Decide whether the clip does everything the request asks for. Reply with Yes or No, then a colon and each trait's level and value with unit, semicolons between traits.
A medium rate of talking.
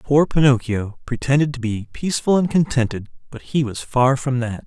Yes: average, 180 wpm